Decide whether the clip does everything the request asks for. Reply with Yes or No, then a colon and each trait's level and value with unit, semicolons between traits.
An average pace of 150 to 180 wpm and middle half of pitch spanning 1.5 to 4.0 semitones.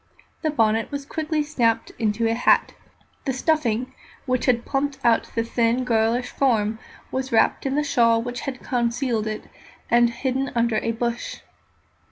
Yes: average, 160 wpm; average, 2.8 semitones